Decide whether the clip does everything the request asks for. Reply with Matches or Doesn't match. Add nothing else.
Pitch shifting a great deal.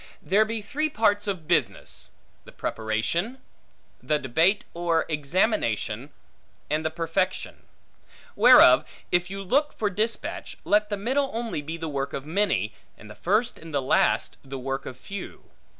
Matches